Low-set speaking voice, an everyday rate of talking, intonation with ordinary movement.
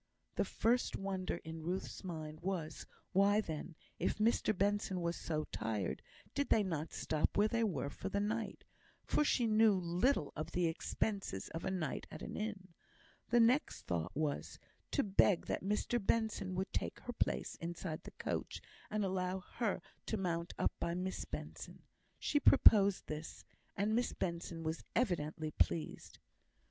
No: medium, 185 Hz; average, 160 wpm; average, 4.6 semitones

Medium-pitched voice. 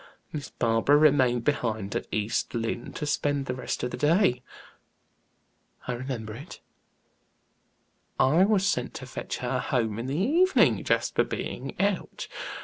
No: low, 130 Hz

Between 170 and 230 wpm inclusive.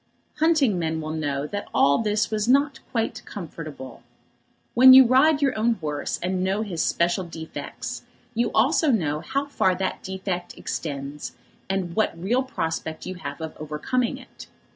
No: average, 160 wpm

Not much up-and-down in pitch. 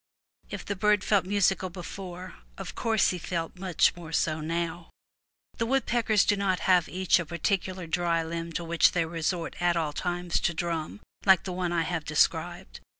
Yes: narrow, 2.3 semitones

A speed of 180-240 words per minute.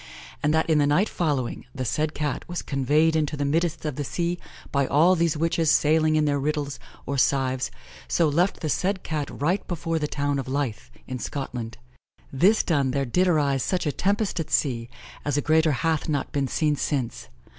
Yes: average, 200 wpm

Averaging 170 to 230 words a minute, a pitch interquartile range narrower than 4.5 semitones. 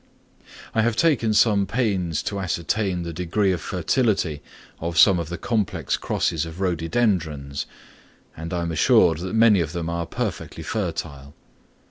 No: average, 150 wpm; average, 4.1 semitones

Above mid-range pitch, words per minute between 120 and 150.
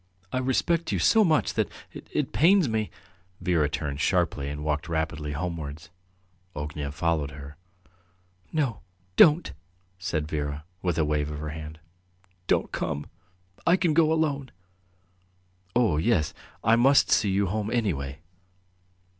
No: very low, 85 Hz; average, 140 wpm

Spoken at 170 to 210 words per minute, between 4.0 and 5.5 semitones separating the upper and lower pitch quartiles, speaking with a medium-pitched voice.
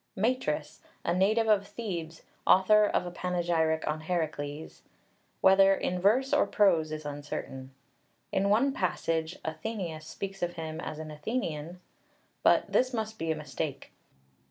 No: average, 140 wpm; average, 4.3 semitones; medium, 175 Hz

